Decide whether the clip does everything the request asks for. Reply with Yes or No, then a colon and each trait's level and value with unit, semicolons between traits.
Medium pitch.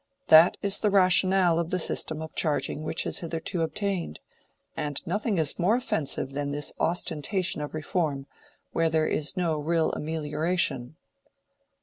Yes: medium, 160 Hz